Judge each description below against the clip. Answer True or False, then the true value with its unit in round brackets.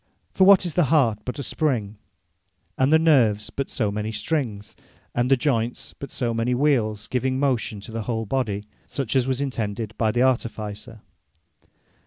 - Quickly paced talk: False (175 wpm)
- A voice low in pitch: True (120 Hz)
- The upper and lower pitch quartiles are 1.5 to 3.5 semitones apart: False (3.9 semitones)